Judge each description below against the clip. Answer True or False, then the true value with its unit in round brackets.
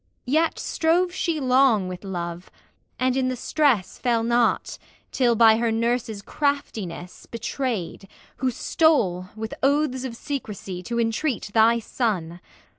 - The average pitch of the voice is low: False (235 Hz)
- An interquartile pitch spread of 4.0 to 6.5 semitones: True (4.5 semitones)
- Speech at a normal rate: False (130 wpm)